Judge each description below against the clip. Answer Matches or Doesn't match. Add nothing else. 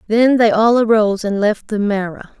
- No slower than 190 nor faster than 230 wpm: Matches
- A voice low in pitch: Doesn't match